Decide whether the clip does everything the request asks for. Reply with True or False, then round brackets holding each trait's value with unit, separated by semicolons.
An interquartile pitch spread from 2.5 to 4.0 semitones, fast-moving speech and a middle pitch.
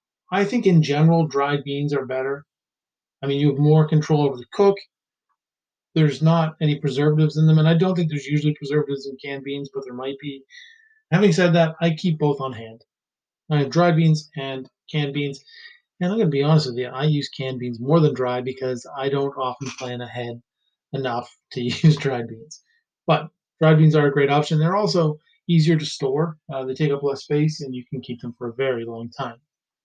True (3.1 semitones; 215 wpm; 145 Hz)